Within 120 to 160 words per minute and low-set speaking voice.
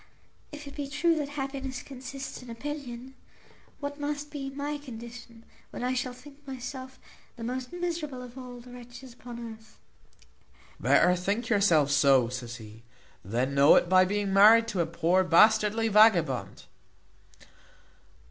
No: average, 150 wpm; high, 240 Hz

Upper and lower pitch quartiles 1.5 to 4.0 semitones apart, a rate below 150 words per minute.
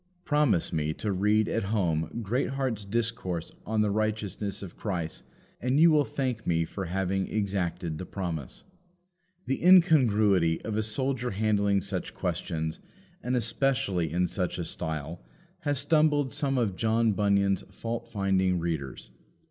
No: average, 4.8 semitones; average, 140 wpm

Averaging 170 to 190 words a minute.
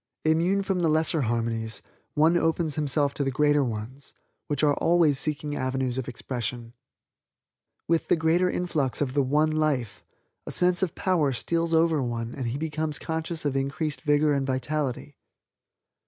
No: average, 160 wpm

